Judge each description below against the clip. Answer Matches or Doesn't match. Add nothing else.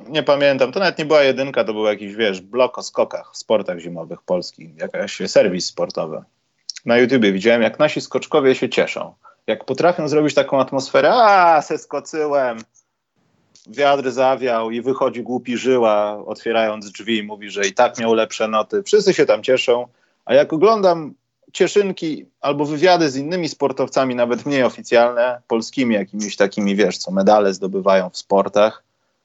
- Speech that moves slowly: Doesn't match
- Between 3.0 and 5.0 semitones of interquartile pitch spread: Doesn't match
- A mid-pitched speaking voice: Doesn't match